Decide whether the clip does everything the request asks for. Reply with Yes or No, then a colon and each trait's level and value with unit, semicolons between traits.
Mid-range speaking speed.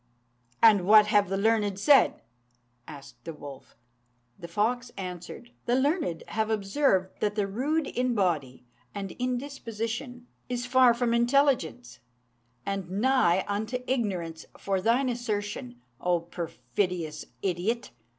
No: slow, 125 wpm